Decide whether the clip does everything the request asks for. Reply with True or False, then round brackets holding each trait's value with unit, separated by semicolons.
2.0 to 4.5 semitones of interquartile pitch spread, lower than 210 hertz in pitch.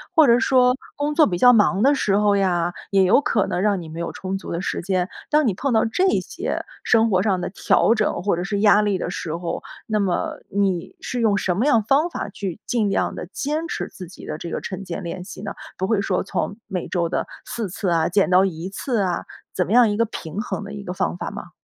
True (3.8 semitones; 200 Hz)